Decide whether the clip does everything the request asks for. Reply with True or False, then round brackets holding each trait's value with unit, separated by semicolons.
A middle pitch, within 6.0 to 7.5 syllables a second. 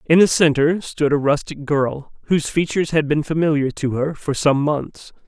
False (150 Hz; 4.9 syllables/s)